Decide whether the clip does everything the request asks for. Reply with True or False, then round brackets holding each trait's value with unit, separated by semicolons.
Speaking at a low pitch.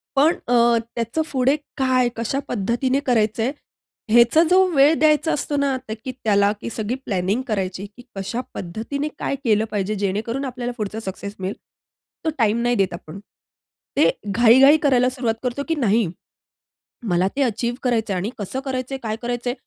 False (235 Hz)